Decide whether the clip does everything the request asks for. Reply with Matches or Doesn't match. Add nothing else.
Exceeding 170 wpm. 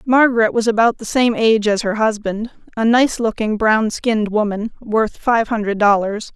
Matches